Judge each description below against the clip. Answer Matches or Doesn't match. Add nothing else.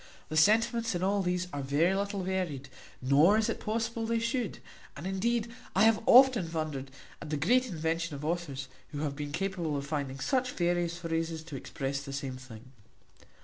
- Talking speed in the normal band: Matches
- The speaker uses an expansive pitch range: Matches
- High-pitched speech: Doesn't match